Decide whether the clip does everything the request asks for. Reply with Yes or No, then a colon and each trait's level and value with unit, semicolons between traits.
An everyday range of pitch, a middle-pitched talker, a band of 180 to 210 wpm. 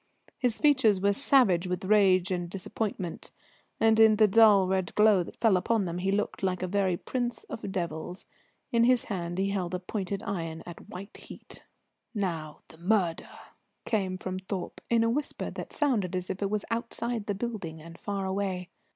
No: average, 3.3 semitones; high, 195 Hz; average, 185 wpm